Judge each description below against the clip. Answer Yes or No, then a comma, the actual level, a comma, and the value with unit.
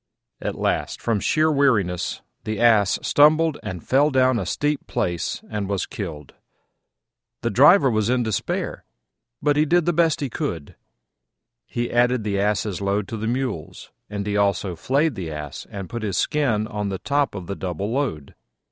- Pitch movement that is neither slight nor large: No, wide, 6.0 semitones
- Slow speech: No, average, 175 wpm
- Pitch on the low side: Yes, low, 110 Hz